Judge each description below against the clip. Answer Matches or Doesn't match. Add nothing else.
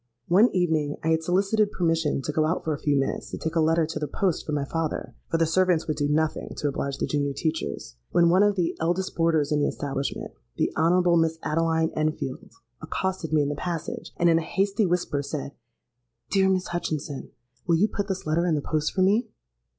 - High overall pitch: Doesn't match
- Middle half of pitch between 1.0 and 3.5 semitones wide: Matches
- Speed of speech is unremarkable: Doesn't match